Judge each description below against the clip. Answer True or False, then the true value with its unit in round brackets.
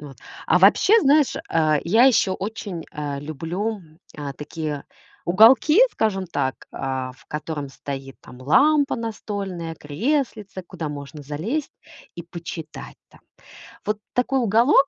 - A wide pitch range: True (7.1 semitones)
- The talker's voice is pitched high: False (175 Hz)